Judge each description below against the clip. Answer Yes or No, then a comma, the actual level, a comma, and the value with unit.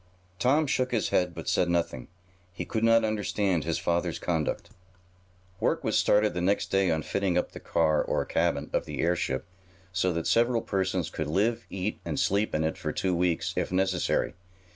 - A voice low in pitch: Yes, very low, 90 Hz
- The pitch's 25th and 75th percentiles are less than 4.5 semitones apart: Yes, average, 3.8 semitones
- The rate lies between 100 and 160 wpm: No, average, 185 wpm